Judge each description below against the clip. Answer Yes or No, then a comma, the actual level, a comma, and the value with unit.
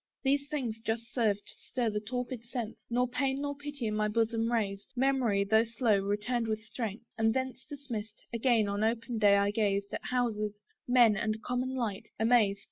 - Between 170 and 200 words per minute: Yes, average, 185 wpm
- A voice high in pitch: Yes, high, 230 Hz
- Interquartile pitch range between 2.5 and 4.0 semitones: Yes, average, 2.9 semitones